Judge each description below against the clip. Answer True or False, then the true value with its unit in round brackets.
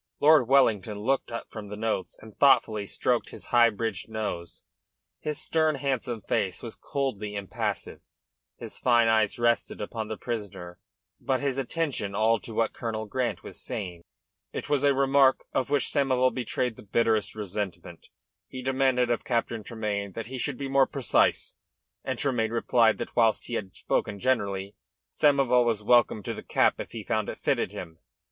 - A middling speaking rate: True (170 wpm)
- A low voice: True (115 Hz)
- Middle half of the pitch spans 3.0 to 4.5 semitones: True (3.8 semitones)